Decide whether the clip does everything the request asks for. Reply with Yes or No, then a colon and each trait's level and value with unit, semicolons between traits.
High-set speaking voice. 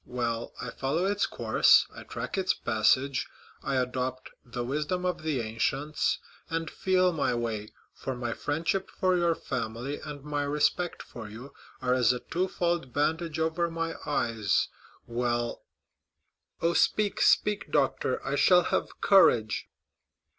No: medium, 145 Hz